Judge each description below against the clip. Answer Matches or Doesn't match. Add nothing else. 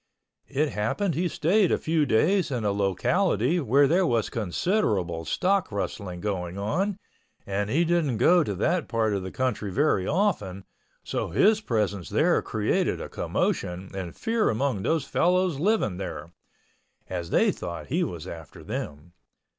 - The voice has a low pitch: Matches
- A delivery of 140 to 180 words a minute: Matches